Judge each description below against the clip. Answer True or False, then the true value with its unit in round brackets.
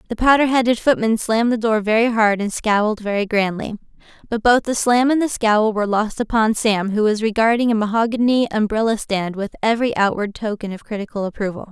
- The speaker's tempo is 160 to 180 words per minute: False (195 wpm)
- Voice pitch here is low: False (220 Hz)